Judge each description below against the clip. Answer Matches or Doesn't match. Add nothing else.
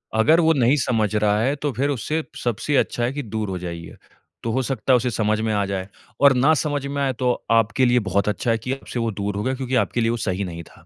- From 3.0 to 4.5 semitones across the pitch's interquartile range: Matches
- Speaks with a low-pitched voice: Matches